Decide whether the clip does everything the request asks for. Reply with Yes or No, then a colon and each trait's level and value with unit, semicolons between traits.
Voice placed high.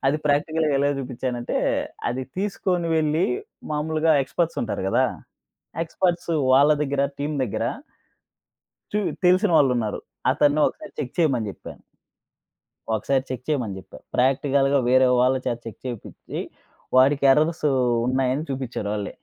No: medium, 140 Hz